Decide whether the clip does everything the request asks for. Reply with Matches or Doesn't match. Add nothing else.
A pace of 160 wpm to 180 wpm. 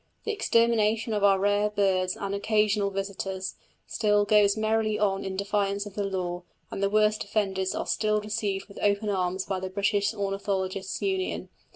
Matches